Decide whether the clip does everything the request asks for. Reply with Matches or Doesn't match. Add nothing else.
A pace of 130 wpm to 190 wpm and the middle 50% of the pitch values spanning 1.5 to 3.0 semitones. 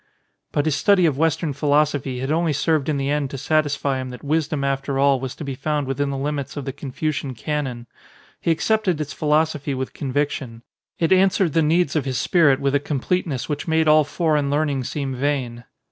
Doesn't match